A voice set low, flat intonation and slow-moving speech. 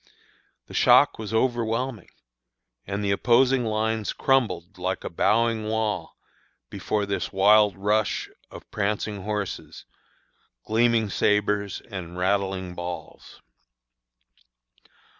Yes: low, 105 Hz; narrow, 2.3 semitones; slow, 100 wpm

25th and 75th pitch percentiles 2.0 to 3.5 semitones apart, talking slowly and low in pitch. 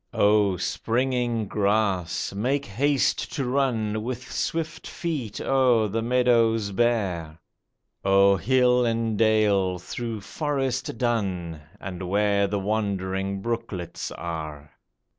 No: average, 4.0 semitones; slow, 105 wpm; low, 110 Hz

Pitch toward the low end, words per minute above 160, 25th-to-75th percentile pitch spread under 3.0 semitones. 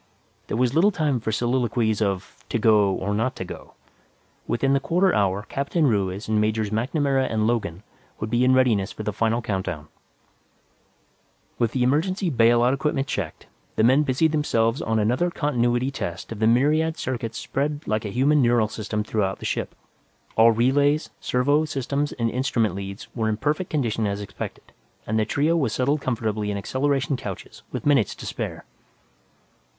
No: low, 120 Hz; average, 175 wpm; average, 4.5 semitones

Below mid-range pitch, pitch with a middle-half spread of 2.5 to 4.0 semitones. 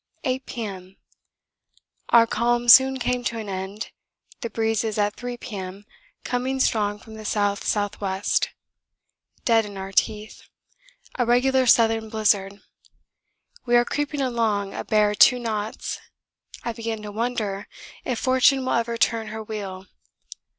No: high, 220 Hz; average, 2.8 semitones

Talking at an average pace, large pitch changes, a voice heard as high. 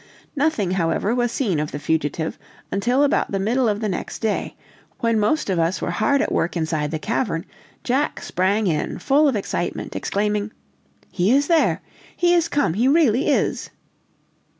Yes: average, 175 wpm; wide, 7.2 semitones; high, 210 Hz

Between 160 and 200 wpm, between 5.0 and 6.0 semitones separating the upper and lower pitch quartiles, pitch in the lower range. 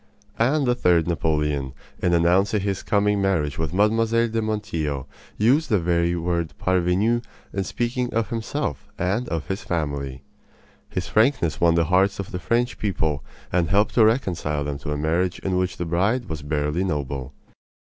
Yes: average, 170 wpm; wide, 5.4 semitones; very low, 90 Hz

